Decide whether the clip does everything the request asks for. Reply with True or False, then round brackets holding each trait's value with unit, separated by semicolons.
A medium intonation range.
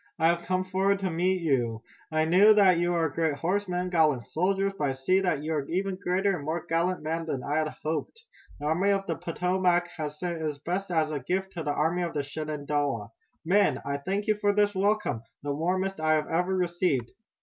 True (3.5 semitones)